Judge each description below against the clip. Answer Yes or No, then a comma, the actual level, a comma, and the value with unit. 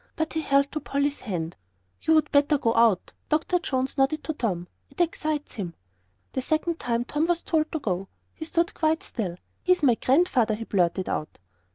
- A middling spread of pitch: No, wide, 5.8 semitones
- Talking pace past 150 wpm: Yes, average, 190 wpm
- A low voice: No, very high, 280 Hz